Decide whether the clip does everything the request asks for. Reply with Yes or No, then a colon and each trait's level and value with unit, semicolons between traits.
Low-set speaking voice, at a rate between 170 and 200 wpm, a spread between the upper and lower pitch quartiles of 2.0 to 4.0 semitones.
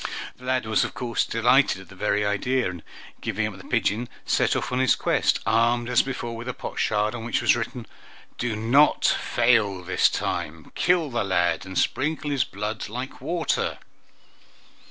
Yes: low, 115 Hz; average, 175 wpm; average, 3.5 semitones